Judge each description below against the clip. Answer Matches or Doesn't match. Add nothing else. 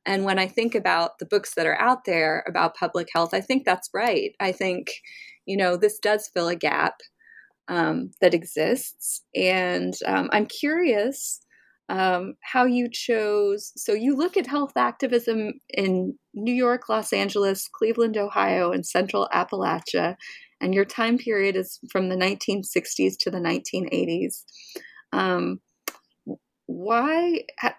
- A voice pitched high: Matches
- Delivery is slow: Doesn't match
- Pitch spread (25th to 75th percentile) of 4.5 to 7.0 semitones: Matches